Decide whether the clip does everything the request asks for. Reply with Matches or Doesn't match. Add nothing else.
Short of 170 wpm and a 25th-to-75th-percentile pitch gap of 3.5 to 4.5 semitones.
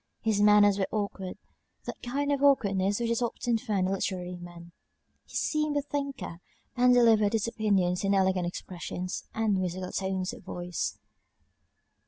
Matches